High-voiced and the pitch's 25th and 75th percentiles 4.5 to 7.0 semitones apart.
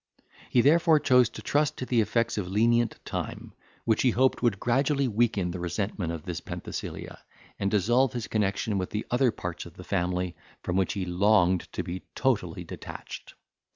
No: low, 105 Hz; average, 5.1 semitones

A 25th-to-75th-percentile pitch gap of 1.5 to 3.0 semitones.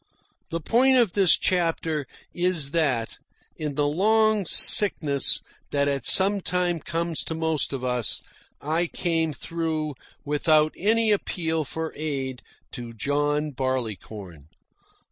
No: average, 3.8 semitones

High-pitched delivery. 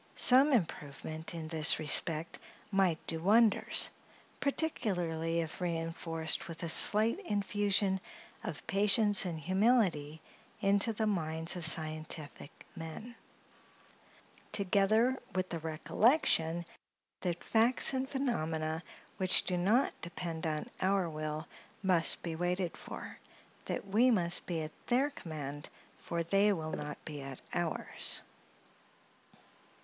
No: medium, 175 Hz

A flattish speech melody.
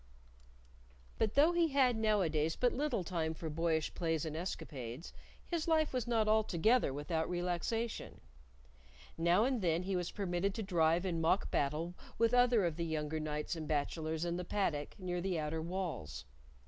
No: average, 5.3 semitones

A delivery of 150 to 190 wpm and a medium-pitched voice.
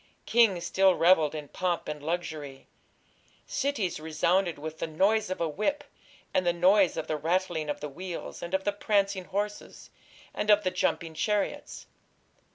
Yes: average, 165 wpm; medium, 180 Hz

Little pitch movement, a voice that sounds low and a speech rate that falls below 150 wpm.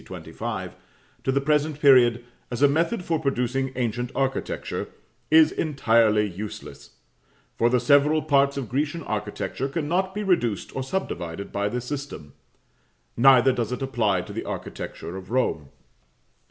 No: average, 4.3 semitones; low, 130 Hz; average, 140 wpm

